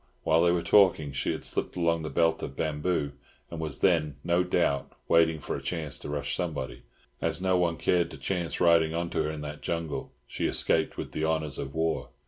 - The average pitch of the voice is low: Yes, very low, 80 Hz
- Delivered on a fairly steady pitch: Yes, narrow, 2.2 semitones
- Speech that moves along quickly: Yes, fast, 215 wpm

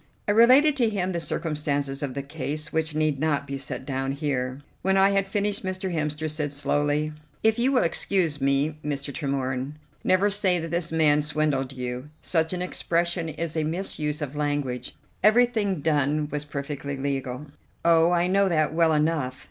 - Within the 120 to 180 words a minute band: Yes, average, 175 wpm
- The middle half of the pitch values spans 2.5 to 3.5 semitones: No, average, 4.0 semitones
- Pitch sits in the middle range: Yes, medium, 155 Hz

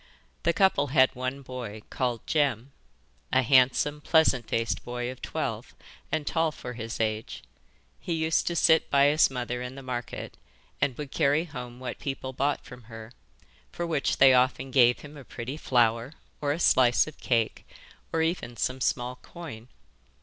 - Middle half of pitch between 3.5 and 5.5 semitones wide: No, average, 3.1 semitones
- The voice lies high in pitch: No, low, 130 Hz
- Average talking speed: Yes, average, 170 wpm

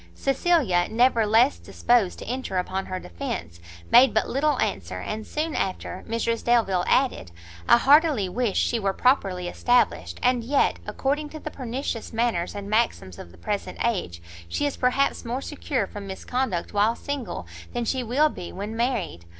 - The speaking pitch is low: No, high, 230 Hz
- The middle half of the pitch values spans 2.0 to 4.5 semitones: No, wide, 5.5 semitones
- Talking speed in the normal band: Yes, average, 165 wpm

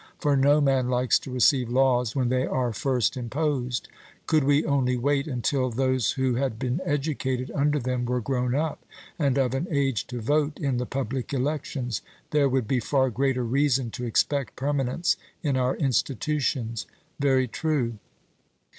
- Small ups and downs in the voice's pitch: Yes, narrow, 2.3 semitones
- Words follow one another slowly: No, average, 165 wpm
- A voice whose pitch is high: No, low, 130 Hz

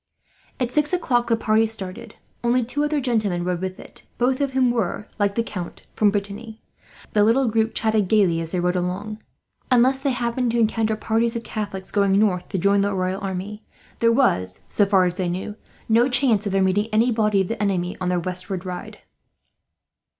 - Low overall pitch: No, high, 215 Hz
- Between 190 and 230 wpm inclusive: Yes, average, 200 wpm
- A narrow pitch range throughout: No, average, 3.8 semitones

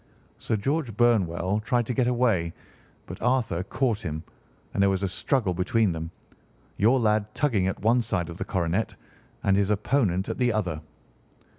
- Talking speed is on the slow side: No, average, 170 wpm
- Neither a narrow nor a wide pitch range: Yes, average, 4.6 semitones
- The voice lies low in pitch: Yes, low, 105 Hz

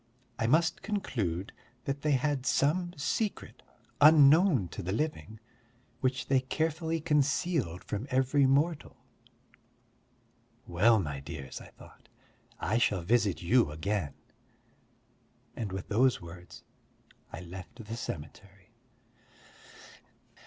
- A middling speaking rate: No, slow, 110 wpm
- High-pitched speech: No, low, 125 Hz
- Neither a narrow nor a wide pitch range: No, wide, 7.8 semitones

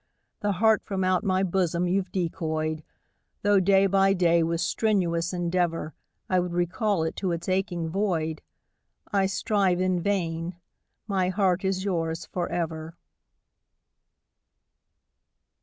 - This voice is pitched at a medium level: Yes, medium, 180 Hz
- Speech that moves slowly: Yes, slow, 125 wpm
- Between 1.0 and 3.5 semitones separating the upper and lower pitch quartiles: Yes, narrow, 2.5 semitones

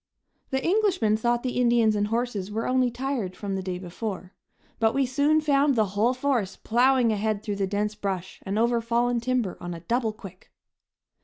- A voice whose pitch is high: Yes, high, 230 Hz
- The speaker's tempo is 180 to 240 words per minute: Yes, average, 185 wpm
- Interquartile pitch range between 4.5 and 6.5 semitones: No, average, 3.8 semitones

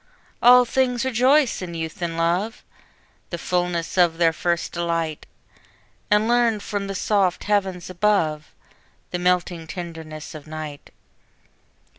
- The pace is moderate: No, slow, 125 wpm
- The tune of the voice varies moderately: Yes, average, 4.1 semitones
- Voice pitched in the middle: Yes, medium, 180 Hz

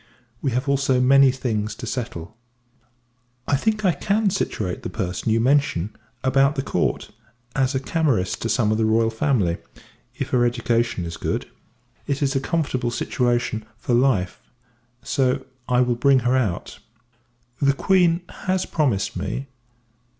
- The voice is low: Yes, low, 125 Hz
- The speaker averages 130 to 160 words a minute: Yes, average, 155 wpm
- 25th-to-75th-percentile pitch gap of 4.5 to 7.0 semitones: No, average, 3.6 semitones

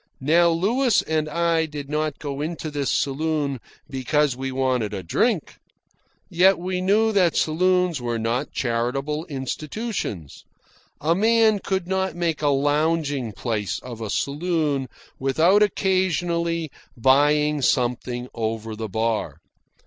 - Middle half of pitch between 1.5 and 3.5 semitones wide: No, average, 5.0 semitones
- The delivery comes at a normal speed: No, slow, 125 wpm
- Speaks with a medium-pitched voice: Yes, medium, 150 Hz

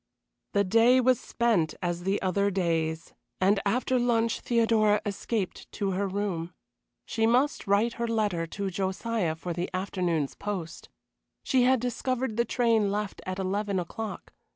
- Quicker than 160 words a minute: No, average, 150 wpm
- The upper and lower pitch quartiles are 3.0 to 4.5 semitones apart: Yes, average, 3.9 semitones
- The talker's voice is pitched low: No, high, 200 Hz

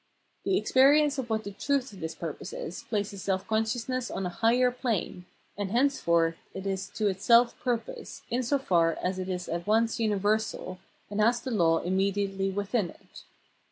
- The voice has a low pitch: No, high, 205 Hz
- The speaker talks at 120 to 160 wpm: No, average, 175 wpm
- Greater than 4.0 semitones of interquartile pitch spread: Yes, average, 4.4 semitones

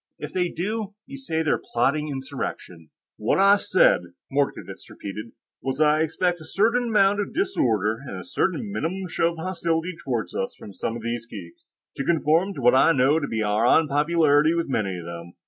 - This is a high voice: No, medium, 150 Hz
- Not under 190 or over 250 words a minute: Yes, average, 195 wpm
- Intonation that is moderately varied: No, wide, 7.6 semitones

